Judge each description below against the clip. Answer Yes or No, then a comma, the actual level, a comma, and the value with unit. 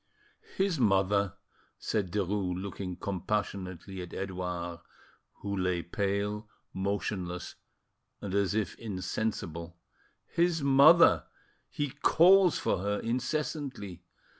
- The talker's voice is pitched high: No, low, 100 Hz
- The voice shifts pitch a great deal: No, average, 3.9 semitones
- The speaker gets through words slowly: Yes, slow, 90 wpm